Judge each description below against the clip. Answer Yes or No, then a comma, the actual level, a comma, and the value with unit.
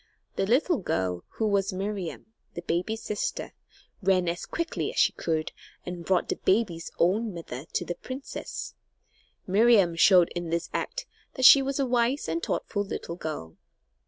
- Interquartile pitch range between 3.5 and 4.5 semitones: No, average, 5.3 semitones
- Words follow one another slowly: No, average, 160 wpm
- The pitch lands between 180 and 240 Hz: Yes, high, 190 Hz